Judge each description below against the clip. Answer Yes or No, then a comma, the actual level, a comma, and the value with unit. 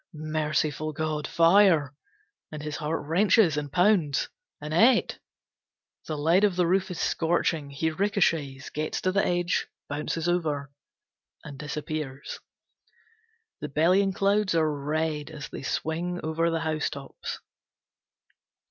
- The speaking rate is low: Yes, slow, 120 wpm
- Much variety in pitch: No, average, 2.9 semitones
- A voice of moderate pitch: Yes, medium, 160 Hz